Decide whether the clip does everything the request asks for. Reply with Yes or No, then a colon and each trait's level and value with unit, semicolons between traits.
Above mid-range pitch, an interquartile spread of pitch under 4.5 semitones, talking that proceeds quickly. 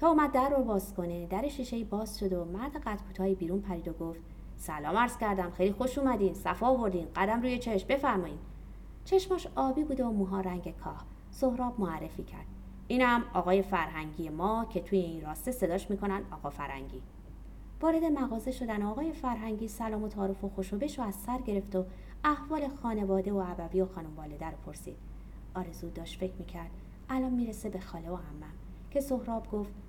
No: high, 200 Hz; wide, 5.6 semitones; fast, 175 wpm